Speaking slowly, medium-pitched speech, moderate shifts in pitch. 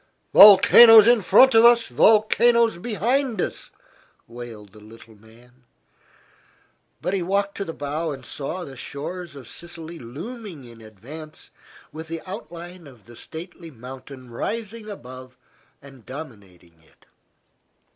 No: slow, 130 wpm; medium, 160 Hz; wide, 8.4 semitones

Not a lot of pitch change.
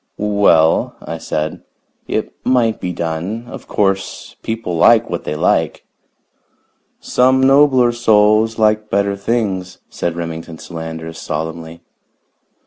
No: wide, 5.5 semitones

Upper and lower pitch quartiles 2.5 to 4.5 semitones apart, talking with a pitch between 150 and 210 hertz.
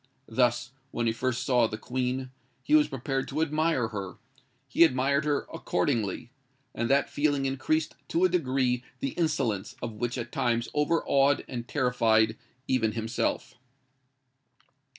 No: average, 3.1 semitones; low, 130 Hz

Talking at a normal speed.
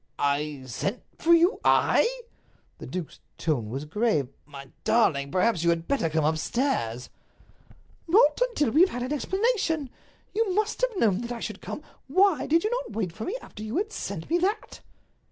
Yes: average, 175 wpm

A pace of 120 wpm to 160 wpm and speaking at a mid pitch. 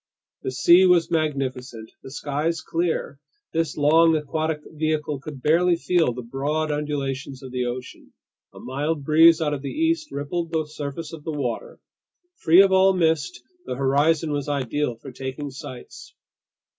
Yes: average, 155 wpm; medium, 150 Hz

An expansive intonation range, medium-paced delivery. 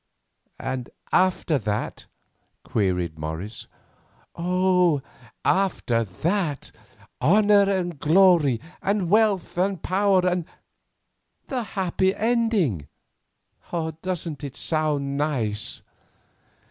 No: wide, 6.4 semitones; slow, 80 wpm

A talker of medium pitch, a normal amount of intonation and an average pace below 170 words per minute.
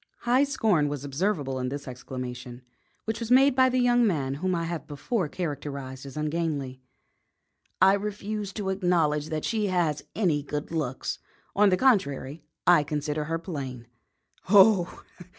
No: medium, 165 Hz; wide, 6.1 semitones; average, 150 wpm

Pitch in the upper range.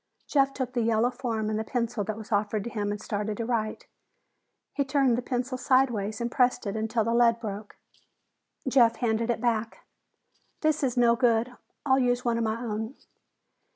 Yes: high, 235 Hz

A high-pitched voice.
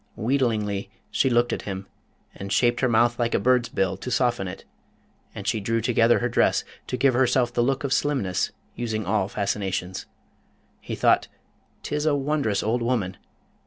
No: low, 120 Hz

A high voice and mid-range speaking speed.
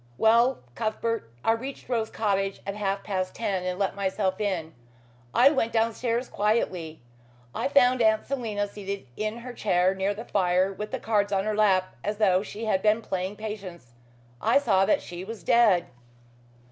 Yes: high, 205 Hz; average, 170 wpm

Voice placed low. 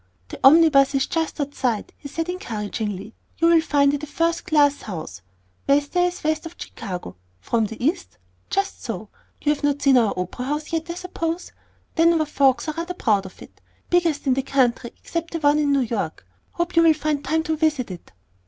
No: very high, 290 Hz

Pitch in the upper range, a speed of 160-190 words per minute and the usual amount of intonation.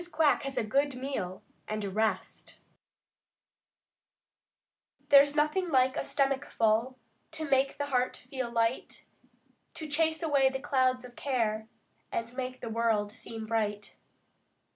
No: very high, 255 Hz; slow, 135 wpm; average, 3.8 semitones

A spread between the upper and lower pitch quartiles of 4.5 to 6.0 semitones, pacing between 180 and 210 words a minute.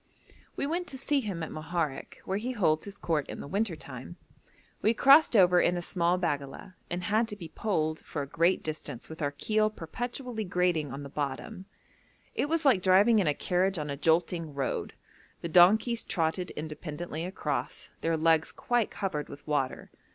Yes: average, 5.2 semitones; average, 185 wpm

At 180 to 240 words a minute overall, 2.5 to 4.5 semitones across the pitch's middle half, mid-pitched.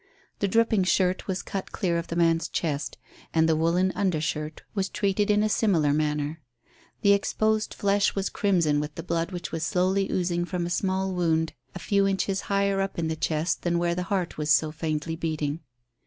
Yes: average, 200 wpm; average, 3.4 semitones; medium, 175 Hz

